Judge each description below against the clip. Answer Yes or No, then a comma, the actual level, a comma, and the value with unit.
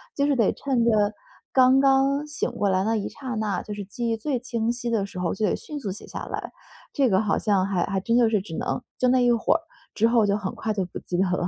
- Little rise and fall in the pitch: No, average, 4.1 semitones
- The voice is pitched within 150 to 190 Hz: No, high, 225 Hz